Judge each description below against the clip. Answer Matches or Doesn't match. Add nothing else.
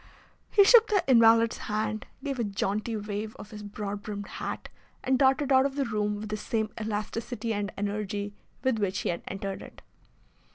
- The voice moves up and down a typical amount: Matches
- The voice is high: Matches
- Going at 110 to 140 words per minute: Doesn't match